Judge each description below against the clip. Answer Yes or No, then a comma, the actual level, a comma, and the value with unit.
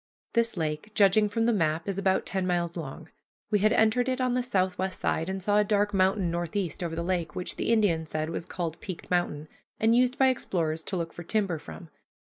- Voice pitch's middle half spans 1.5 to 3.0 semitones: No, average, 4.1 semitones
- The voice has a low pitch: No, medium, 185 Hz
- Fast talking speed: Yes, fast, 220 wpm